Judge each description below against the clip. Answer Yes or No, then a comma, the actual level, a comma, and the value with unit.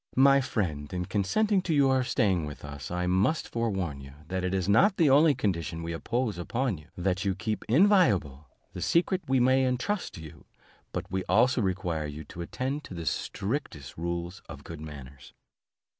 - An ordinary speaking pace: Yes, average, 185 wpm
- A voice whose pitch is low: Yes, very low, 95 Hz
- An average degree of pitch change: No, wide, 7.7 semitones